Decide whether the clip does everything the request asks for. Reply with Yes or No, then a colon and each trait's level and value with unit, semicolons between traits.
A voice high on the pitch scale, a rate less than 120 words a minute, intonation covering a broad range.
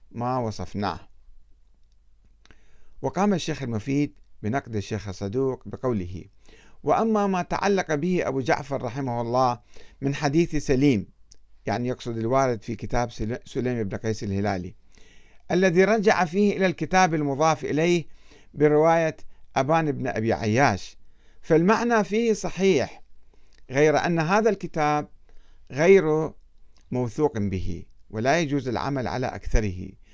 No: low, 135 Hz; average, 110 wpm; wide, 7.0 semitones